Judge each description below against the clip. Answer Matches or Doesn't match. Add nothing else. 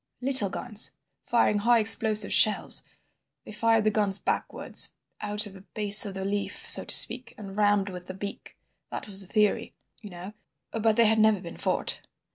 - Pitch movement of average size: Doesn't match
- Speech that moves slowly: Doesn't match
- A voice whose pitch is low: Doesn't match